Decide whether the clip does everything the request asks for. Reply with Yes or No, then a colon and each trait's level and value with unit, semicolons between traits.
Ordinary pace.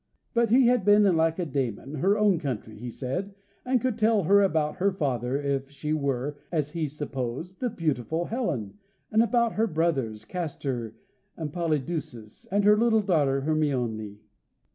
Yes: average, 160 wpm